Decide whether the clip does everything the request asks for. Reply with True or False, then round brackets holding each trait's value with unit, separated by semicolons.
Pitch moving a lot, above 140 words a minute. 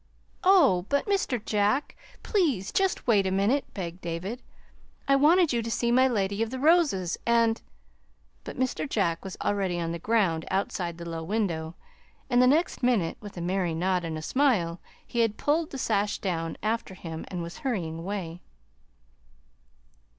True (6.4 semitones; 170 wpm)